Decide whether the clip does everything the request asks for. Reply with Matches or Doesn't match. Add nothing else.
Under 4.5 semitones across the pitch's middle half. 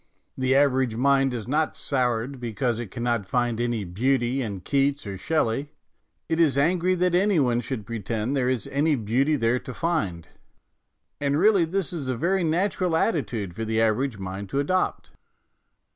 Doesn't match